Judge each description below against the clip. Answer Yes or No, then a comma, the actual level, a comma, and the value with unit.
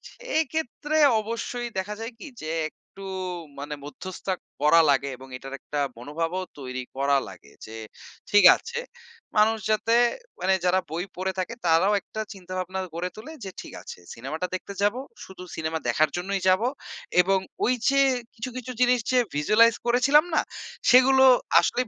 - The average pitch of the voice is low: No, high, 190 Hz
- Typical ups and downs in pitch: No, wide, 6.7 semitones